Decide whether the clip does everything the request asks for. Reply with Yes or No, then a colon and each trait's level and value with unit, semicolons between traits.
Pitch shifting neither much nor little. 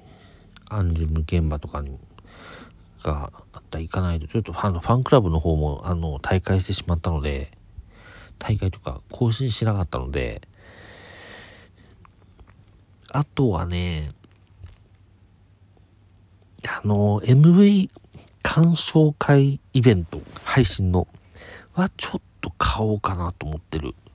Yes: average, 3.6 semitones